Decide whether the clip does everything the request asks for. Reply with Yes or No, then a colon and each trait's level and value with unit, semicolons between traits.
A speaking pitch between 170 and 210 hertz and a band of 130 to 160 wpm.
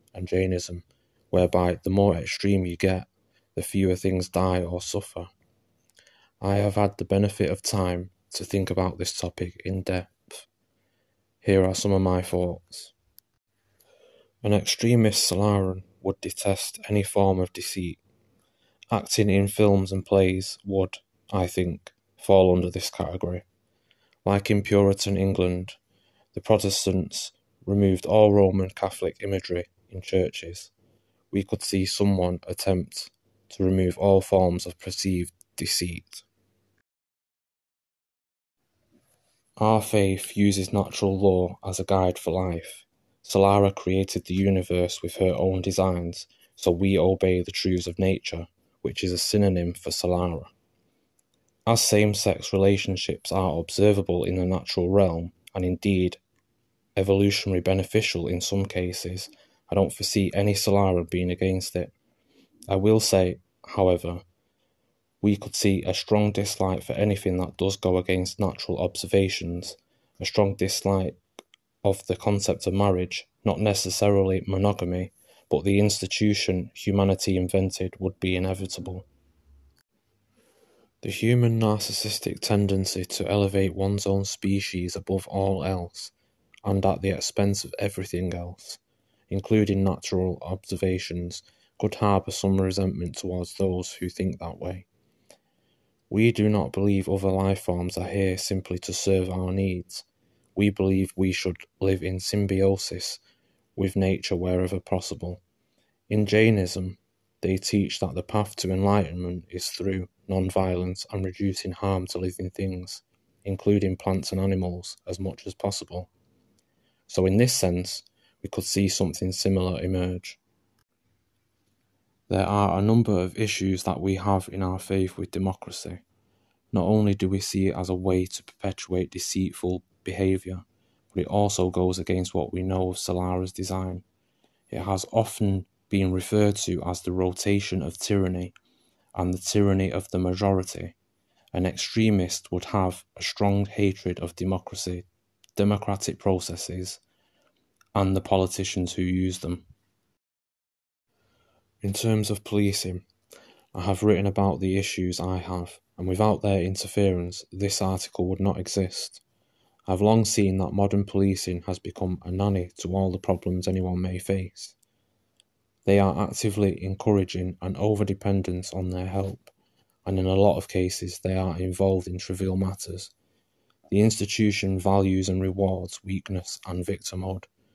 No: very low, 95 Hz; slow, 135 wpm